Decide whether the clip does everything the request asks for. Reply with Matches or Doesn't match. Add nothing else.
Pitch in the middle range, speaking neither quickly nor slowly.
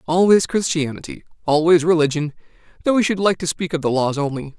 Matches